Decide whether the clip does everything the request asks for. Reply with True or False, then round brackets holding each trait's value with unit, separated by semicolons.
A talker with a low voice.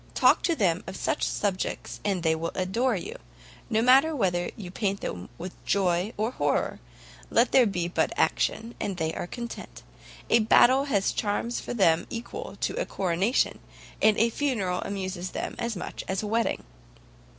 False (200 Hz)